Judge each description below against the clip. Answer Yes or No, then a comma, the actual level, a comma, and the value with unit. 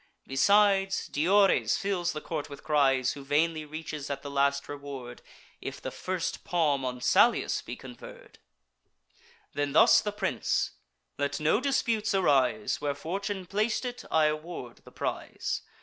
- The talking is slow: No, average, 145 wpm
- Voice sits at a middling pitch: Yes, medium, 155 Hz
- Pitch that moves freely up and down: Yes, wide, 5.8 semitones